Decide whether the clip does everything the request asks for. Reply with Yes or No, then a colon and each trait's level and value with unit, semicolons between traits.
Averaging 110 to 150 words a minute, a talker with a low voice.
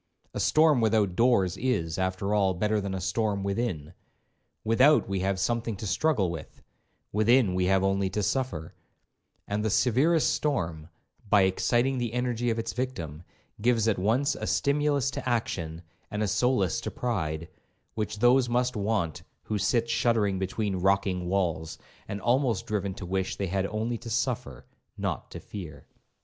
No: average, 160 wpm; low, 105 Hz